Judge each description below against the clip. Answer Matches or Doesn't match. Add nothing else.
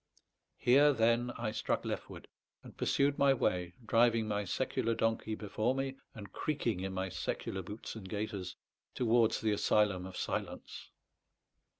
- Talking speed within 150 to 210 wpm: Doesn't match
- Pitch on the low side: Matches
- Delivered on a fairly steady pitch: Doesn't match